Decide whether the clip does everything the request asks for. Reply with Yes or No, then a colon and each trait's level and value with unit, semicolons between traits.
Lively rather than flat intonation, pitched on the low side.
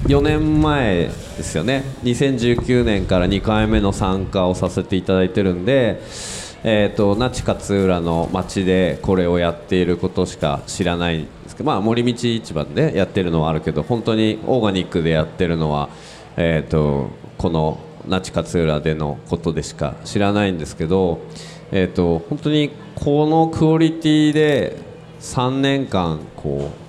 Yes: wide, 6.1 semitones; very low, 95 Hz